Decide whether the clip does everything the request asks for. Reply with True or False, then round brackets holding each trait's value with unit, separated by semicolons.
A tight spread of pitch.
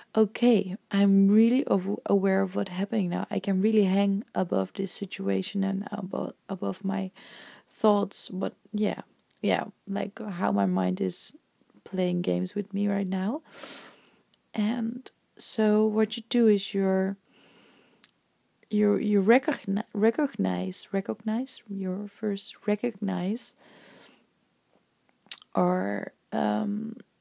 True (2.2 semitones)